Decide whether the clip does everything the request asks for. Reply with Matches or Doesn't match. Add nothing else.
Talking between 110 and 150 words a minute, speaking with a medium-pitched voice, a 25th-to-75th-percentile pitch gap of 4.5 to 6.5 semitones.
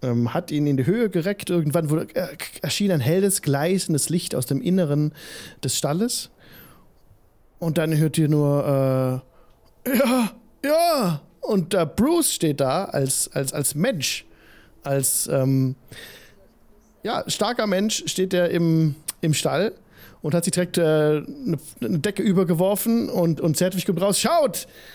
Matches